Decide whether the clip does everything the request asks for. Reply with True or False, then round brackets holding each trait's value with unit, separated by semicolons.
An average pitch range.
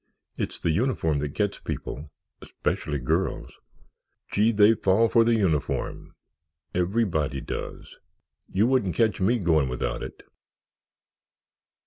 False (6.8 semitones)